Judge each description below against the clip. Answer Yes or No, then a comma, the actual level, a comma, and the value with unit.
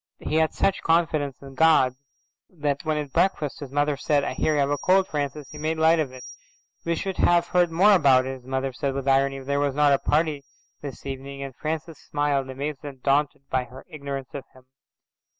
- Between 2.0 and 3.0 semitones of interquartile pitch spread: Yes, narrow, 2.6 semitones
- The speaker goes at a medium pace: No, fast, 220 wpm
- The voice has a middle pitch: Yes, medium, 145 Hz